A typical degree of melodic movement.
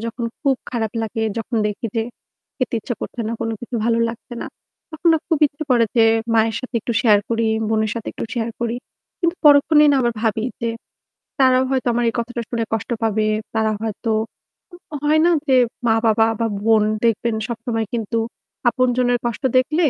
No: narrow, 2.2 semitones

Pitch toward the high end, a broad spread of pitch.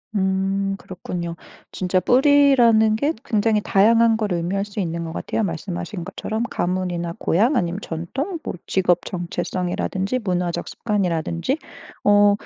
No: high, 195 Hz; average, 3.9 semitones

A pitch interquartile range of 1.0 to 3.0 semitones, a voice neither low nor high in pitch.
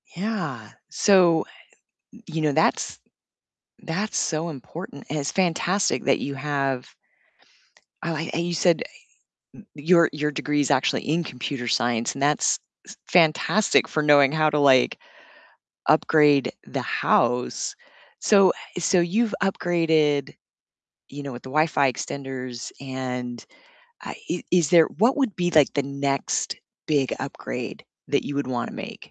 No: average, 4.0 semitones; medium, 150 Hz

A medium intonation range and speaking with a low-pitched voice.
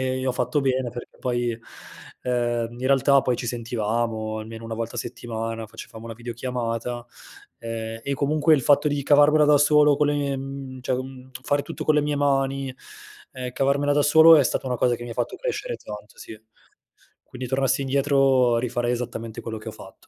Yes: average, 3.1 semitones; low, 130 Hz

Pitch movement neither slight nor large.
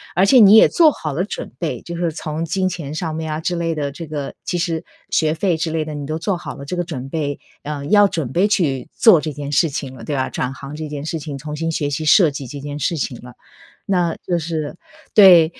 Yes: average, 3.3 semitones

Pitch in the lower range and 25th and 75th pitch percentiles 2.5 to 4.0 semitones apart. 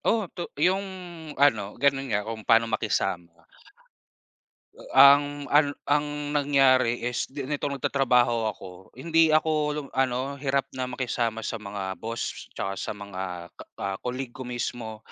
No: low, 125 Hz; average, 4.5 semitones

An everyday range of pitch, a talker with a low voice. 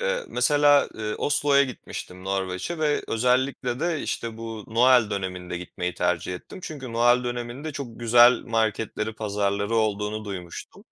Yes: average, 4.3 semitones; low, 115 Hz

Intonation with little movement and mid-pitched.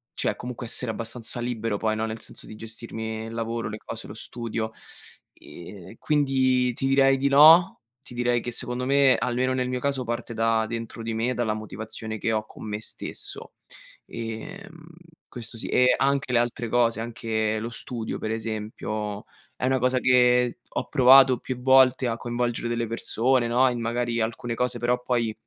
No: narrow, 2.0 semitones; low, 120 Hz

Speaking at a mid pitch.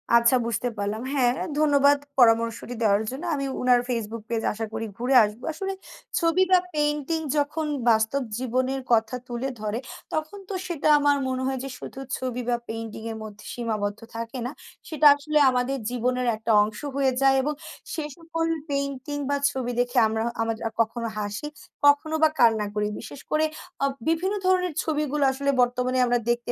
No: very high, 255 Hz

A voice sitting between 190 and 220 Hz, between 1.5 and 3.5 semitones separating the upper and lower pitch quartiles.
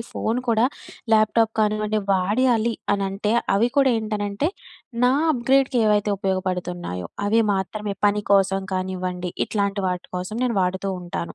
Yes: high, 205 Hz; average, 2.9 semitones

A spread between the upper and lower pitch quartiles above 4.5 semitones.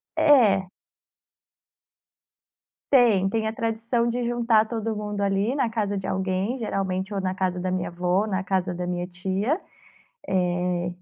No: average, 3.5 semitones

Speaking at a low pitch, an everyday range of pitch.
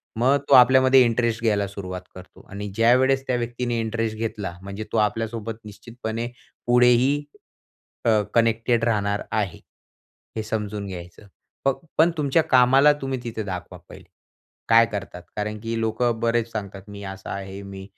Yes: low, 115 Hz; average, 3.0 semitones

